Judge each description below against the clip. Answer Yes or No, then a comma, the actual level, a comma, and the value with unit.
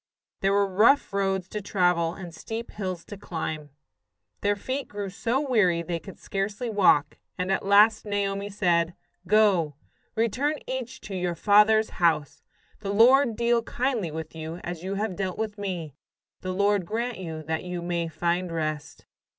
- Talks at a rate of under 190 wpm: Yes, average, 165 wpm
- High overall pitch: Yes, high, 195 Hz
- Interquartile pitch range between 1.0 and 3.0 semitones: No, average, 3.9 semitones